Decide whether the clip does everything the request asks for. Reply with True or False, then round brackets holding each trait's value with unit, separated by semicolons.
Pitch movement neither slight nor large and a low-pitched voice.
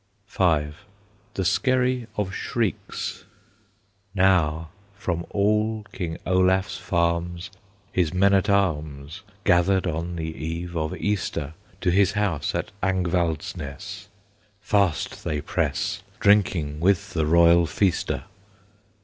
True (3.4 semitones; 90 Hz)